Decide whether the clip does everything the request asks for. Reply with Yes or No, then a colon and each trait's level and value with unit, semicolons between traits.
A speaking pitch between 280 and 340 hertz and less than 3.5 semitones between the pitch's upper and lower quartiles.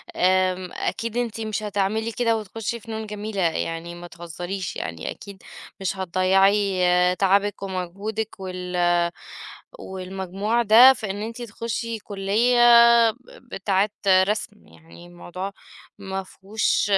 No: high, 195 Hz; average, 2.8 semitones